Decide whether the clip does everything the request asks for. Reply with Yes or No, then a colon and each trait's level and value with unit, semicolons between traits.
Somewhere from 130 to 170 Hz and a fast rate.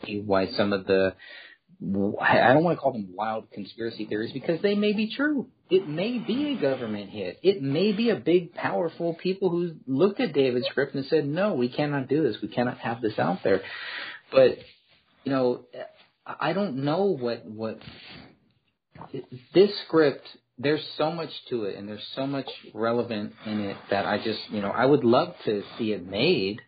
No: low, 135 Hz; average, 185 wpm